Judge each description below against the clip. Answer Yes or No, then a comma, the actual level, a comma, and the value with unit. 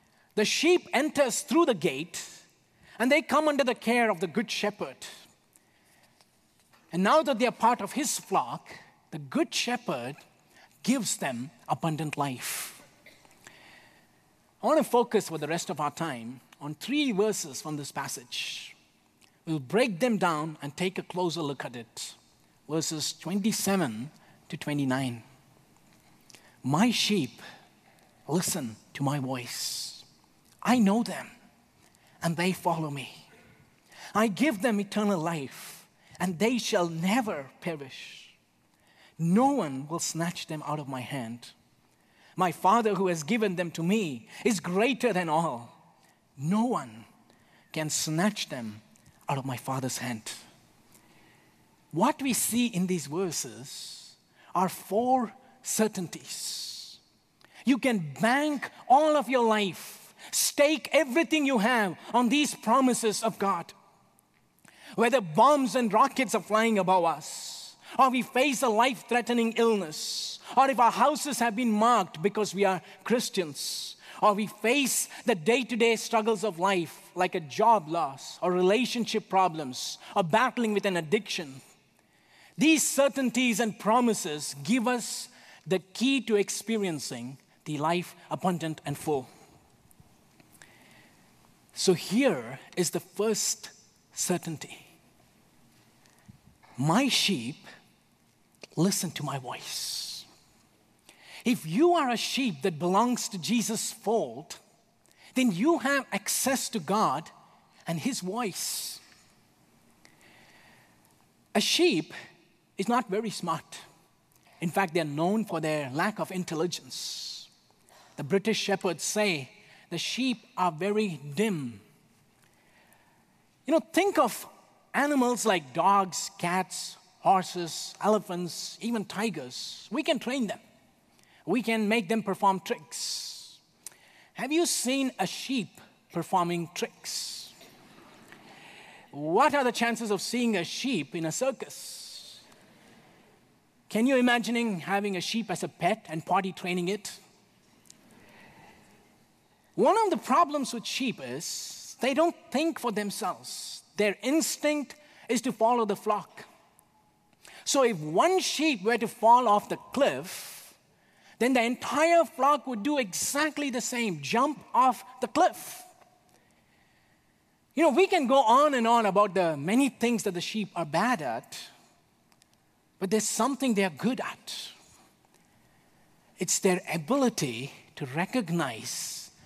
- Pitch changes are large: Yes, wide, 6.1 semitones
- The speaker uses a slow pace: Yes, slow, 130 wpm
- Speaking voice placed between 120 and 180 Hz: No, high, 205 Hz